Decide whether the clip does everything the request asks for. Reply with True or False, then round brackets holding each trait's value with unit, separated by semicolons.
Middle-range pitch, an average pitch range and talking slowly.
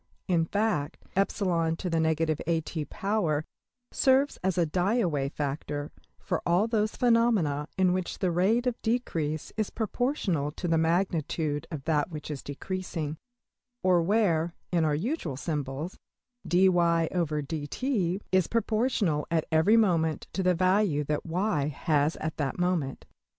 True (170 Hz; 4.3 semitones; 125 wpm)